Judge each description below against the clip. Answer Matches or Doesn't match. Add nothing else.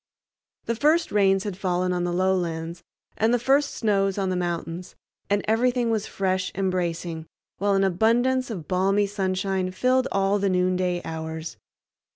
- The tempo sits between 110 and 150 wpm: Doesn't match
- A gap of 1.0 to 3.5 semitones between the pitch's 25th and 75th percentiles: Matches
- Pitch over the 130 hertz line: Matches